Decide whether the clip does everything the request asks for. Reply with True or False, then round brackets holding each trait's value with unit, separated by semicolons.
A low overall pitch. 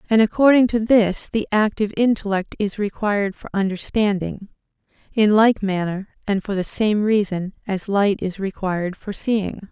False (205 Hz)